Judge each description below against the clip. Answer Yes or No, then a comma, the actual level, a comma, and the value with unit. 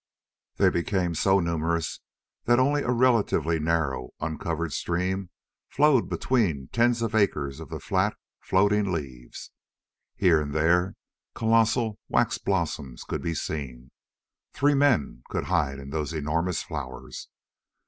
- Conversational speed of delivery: No, slow, 130 wpm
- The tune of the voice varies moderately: No, wide, 6.4 semitones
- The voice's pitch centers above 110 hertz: No, very low, 85 Hz